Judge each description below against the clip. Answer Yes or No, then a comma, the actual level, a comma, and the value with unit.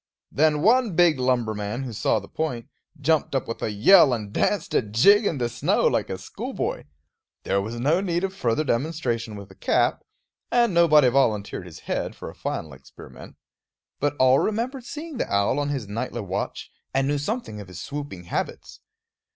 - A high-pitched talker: No, low, 135 Hz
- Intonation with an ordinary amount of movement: No, wide, 7.4 semitones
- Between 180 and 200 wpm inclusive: Yes, average, 185 wpm